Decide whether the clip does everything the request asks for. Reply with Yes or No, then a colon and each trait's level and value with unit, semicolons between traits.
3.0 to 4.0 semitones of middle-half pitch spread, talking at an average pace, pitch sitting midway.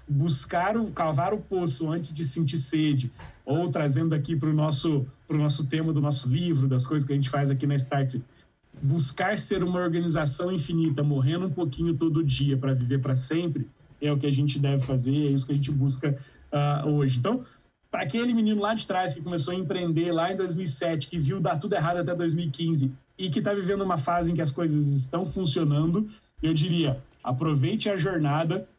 No: average, 3.5 semitones; fast, 200 wpm; medium, 155 Hz